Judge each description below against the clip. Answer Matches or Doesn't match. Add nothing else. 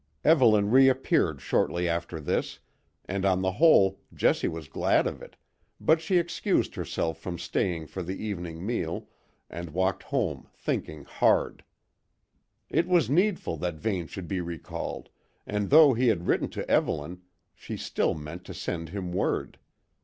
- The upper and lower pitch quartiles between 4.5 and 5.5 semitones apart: Matches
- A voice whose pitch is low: Matches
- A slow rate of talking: Doesn't match